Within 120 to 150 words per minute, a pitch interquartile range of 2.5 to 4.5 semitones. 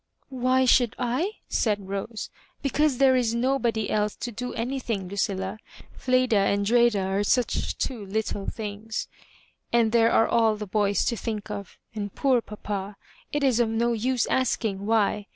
No: average, 160 wpm; average, 3.3 semitones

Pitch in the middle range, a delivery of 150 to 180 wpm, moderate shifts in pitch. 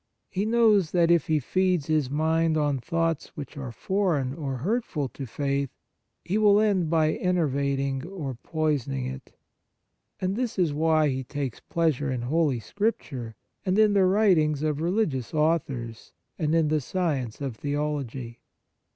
Yes: medium, 155 Hz; average, 155 wpm; average, 4.6 semitones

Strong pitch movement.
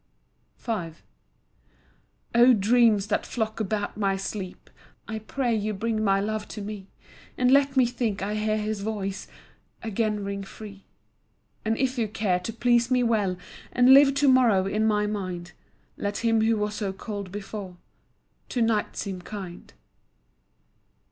No: narrow, 2.6 semitones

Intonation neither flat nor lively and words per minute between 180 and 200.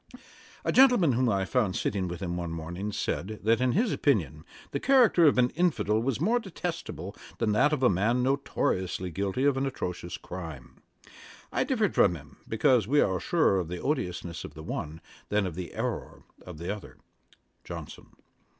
No: wide, 7.4 semitones; average, 185 wpm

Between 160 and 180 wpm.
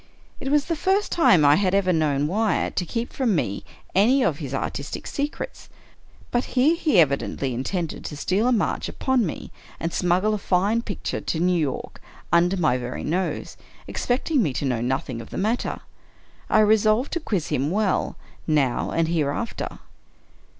Yes: average, 175 wpm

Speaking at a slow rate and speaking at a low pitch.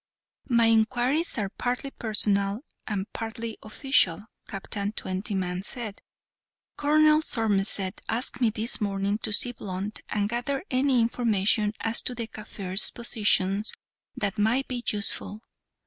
No: slow, 125 wpm; high, 220 Hz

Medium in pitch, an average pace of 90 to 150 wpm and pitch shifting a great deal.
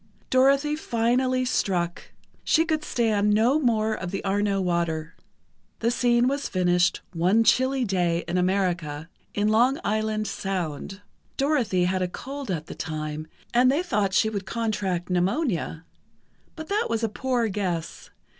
No: high, 210 Hz; average, 145 wpm; wide, 5.9 semitones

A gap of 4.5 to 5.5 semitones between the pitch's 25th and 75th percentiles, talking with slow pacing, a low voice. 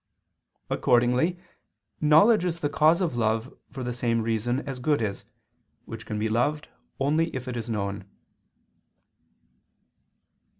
Yes: average, 5.1 semitones; slow, 120 wpm; low, 125 Hz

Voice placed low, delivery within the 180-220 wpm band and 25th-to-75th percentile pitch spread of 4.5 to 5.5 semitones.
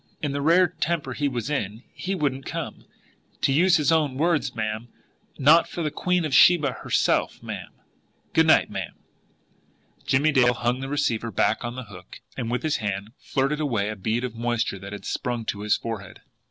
Yes: low, 130 Hz; average, 190 wpm; average, 5.1 semitones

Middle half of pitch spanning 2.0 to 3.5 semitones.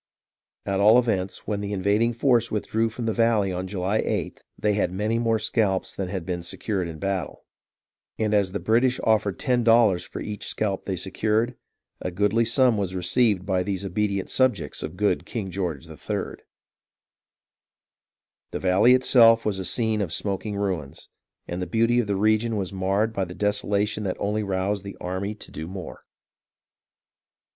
Yes: average, 3.0 semitones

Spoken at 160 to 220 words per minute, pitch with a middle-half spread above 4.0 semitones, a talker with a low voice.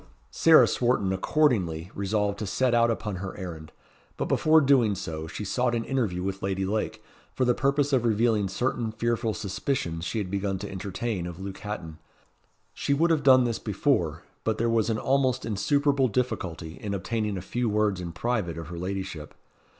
Yes: average, 180 wpm; average, 4.4 semitones; low, 105 Hz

